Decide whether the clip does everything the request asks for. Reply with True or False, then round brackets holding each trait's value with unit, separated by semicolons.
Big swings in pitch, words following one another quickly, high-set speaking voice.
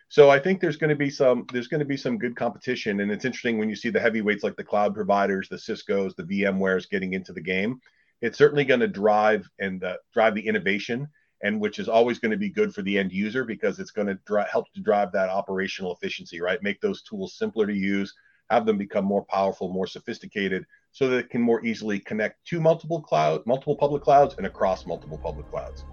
False (6.6 semitones; 230 wpm; 115 Hz)